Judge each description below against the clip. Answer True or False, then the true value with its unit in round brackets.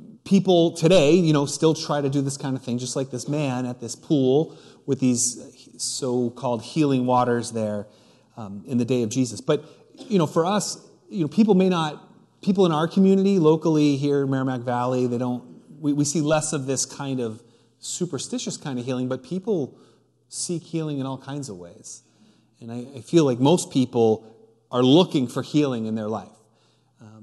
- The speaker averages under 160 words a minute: False (190 wpm)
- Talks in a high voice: False (135 Hz)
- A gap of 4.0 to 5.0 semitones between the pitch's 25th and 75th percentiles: True (4.6 semitones)